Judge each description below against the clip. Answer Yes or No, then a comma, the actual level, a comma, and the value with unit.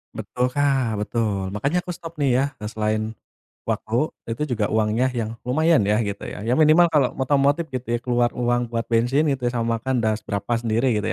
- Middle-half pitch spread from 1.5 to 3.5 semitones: No, average, 3.9 semitones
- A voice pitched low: Yes, low, 120 Hz